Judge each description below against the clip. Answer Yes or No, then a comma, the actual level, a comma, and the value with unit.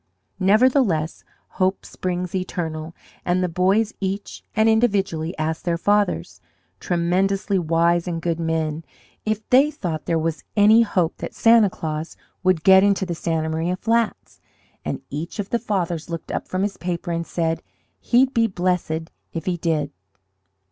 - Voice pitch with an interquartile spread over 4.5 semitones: No, average, 3.6 semitones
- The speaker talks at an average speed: Yes, average, 155 wpm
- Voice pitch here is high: No, medium, 180 Hz